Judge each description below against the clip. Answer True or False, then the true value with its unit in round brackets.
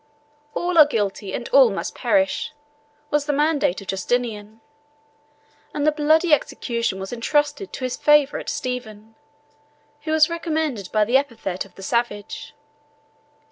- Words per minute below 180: True (140 wpm)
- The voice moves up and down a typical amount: False (6.1 semitones)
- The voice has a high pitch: True (255 Hz)